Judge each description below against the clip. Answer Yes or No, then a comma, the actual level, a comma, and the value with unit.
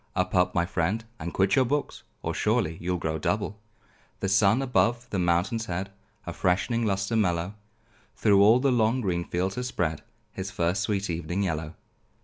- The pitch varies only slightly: No, average, 4.2 semitones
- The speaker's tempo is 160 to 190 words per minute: Yes, average, 175 wpm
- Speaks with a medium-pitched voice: No, very low, 95 Hz